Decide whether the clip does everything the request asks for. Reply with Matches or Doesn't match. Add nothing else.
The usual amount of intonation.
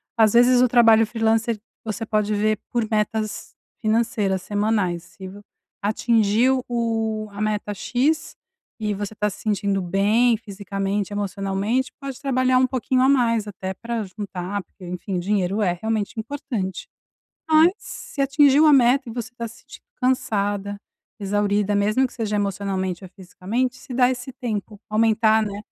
Matches